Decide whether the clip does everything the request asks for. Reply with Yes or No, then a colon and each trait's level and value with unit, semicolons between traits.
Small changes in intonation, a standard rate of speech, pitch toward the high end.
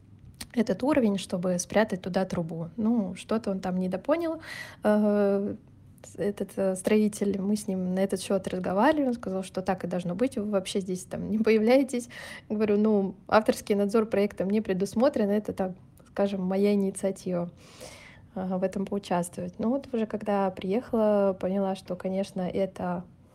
Yes: narrow, 2.3 semitones; average, 145 wpm; high, 200 Hz